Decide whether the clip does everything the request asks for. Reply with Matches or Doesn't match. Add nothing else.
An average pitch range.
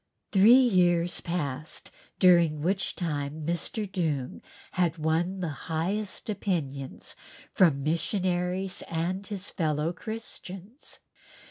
Matches